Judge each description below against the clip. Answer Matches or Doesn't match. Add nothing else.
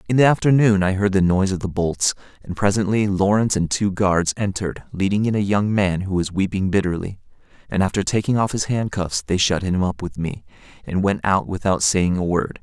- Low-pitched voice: Matches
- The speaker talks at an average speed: Doesn't match